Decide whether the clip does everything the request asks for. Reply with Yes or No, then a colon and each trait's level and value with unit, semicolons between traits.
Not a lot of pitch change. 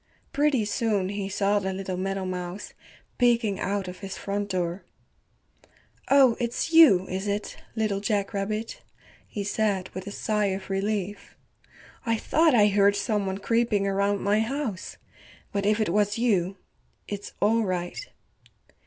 Yes: narrow, 2.1 semitones